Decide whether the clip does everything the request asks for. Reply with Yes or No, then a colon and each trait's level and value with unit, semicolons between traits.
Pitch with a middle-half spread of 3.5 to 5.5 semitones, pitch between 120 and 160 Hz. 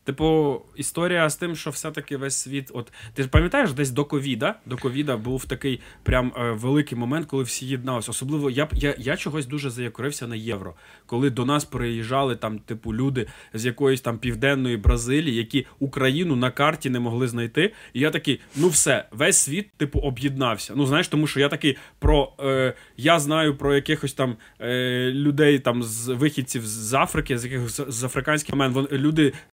No: average, 3.0 semitones; low, 135 Hz